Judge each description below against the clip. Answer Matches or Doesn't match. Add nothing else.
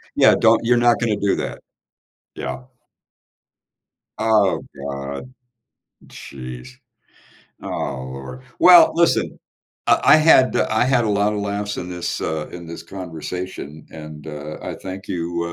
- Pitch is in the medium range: Doesn't match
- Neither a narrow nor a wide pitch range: Doesn't match